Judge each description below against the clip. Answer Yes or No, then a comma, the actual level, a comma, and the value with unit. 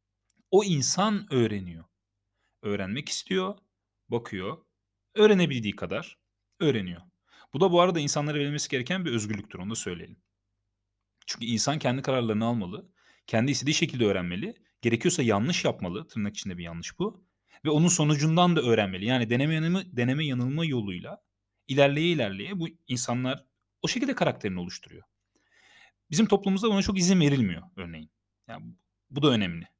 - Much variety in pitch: Yes, wide, 8.2 semitones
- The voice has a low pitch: Yes, low, 125 Hz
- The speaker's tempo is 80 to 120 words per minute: No, average, 135 wpm